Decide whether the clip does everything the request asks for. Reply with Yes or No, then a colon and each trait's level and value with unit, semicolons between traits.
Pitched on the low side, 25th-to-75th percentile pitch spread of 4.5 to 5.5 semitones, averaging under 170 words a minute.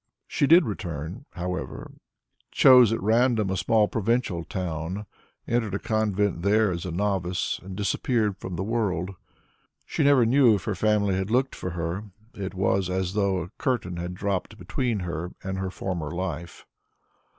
No: very low, 95 Hz; average, 3.3 semitones; average, 160 wpm